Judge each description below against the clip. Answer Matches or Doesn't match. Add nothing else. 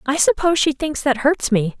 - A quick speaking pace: Matches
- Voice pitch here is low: Doesn't match